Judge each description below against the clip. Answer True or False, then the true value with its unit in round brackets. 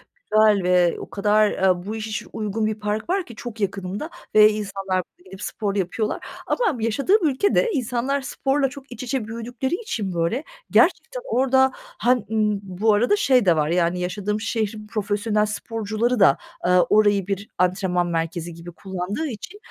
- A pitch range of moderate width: True (4.3 semitones)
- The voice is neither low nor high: False (215 Hz)